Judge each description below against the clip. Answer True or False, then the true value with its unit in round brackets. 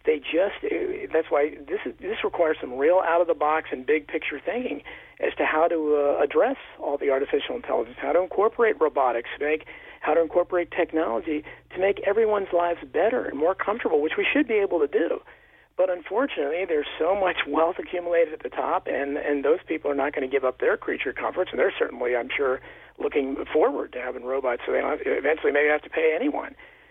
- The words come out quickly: True (215 wpm)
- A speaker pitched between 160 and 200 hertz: True (185 Hz)